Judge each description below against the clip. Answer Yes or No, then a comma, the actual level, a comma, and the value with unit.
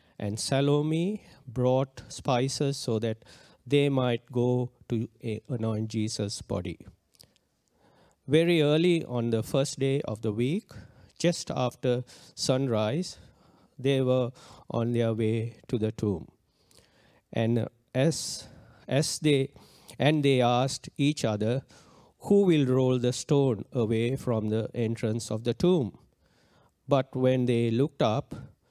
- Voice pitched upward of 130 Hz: No, low, 125 Hz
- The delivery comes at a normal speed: No, slow, 125 wpm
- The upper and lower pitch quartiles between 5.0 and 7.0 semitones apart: No, average, 3.6 semitones